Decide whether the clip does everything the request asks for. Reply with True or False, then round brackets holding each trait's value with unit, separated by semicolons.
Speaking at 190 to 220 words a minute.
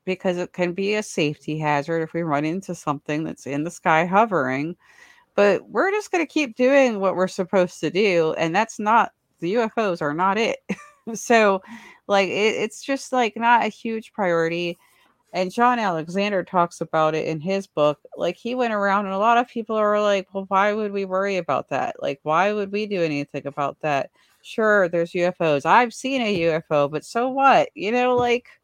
True (195 wpm)